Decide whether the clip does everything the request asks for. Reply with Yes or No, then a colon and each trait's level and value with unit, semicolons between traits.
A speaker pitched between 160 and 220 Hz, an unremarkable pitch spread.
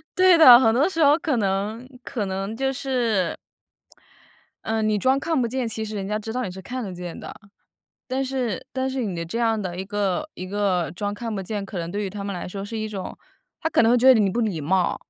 Yes: high, 215 Hz; average, 4.7 semitones